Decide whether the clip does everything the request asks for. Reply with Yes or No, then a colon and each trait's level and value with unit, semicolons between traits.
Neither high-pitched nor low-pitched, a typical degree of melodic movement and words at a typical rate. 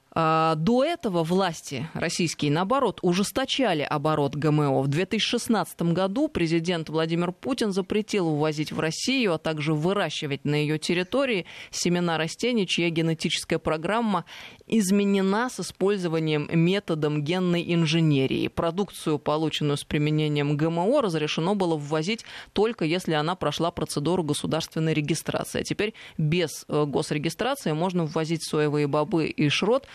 Yes: medium, 165 Hz; average, 4.1 semitones; average, 120 wpm